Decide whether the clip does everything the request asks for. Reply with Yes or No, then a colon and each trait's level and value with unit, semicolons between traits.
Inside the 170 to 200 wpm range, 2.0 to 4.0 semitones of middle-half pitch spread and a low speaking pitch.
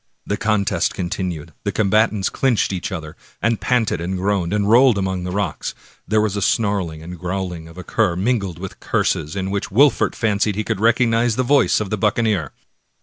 Yes: average, 195 wpm; average, 3.3 semitones; low, 100 Hz